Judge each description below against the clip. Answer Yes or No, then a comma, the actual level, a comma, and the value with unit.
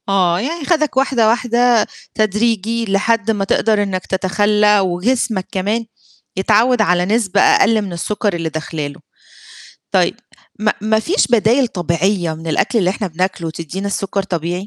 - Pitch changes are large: No, average, 3.7 semitones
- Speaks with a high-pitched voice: Yes, high, 205 Hz